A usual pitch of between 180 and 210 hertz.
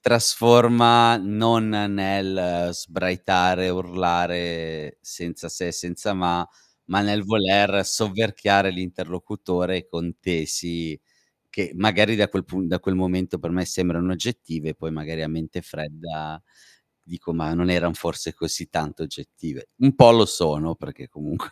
No: very low, 90 Hz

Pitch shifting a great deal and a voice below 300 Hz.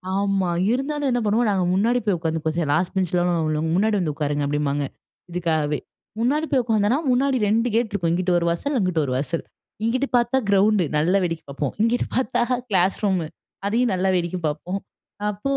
Yes: wide, 5.7 semitones; high, 190 Hz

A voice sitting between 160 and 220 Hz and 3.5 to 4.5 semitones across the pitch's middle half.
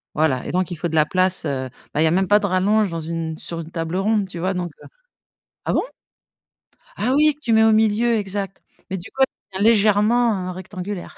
Yes: high, 190 Hz; average, 4.0 semitones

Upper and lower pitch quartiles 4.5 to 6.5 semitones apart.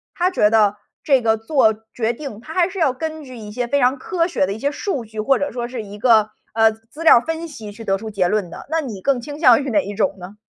Yes: average, 5.0 semitones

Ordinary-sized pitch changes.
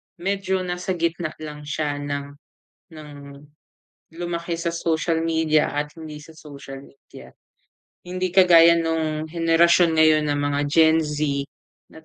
No: narrow, 2.1 semitones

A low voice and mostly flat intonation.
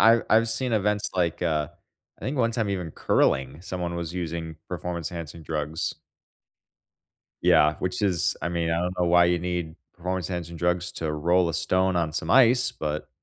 Yes: very low, 85 Hz; narrow, 2.2 semitones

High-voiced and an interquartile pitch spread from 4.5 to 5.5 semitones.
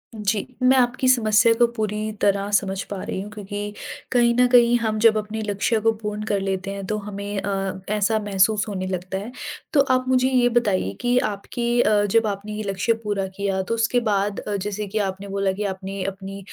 No: high, 205 Hz; narrow, 2.5 semitones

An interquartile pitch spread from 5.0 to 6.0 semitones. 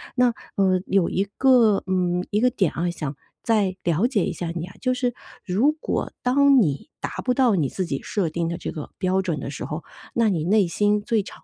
Yes: wide, 5.5 semitones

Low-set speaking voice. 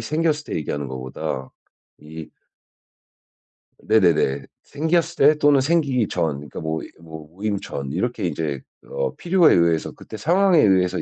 Yes: very low, 95 Hz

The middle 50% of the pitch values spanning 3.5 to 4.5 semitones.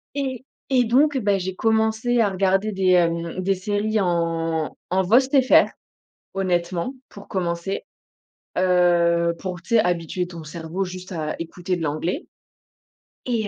Yes: average, 4.1 semitones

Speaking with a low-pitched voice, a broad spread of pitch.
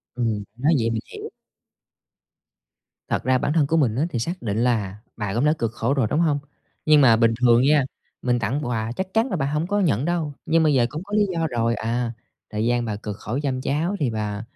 No: low, 125 Hz; average, 4.9 semitones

